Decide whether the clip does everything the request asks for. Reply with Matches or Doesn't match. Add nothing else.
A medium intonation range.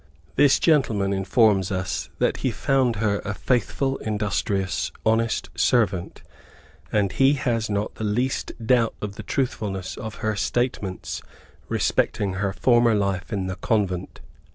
Matches